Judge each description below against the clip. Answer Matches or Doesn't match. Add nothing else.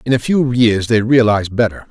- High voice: Doesn't match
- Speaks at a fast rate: Matches